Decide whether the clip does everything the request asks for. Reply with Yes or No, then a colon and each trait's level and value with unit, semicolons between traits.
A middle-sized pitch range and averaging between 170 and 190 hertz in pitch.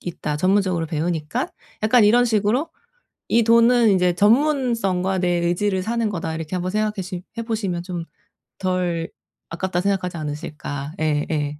Yes: average, 4.4 semitones; medium, 185 Hz